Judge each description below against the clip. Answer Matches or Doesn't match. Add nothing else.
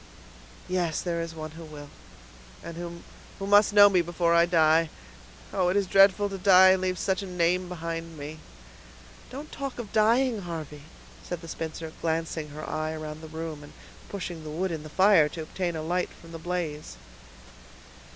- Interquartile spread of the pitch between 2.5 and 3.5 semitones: Matches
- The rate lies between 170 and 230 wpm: Matches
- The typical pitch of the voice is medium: Matches